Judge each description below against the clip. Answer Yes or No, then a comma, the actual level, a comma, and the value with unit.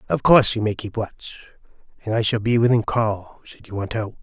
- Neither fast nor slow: No, fast, 225 wpm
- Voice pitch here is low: Yes, low, 110 Hz